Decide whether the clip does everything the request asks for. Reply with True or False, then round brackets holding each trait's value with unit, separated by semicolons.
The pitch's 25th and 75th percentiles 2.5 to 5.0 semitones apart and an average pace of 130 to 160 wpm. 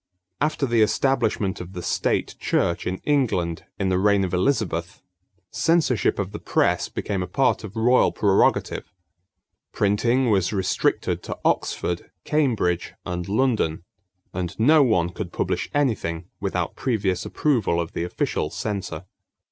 False (5.6 semitones; 140 wpm)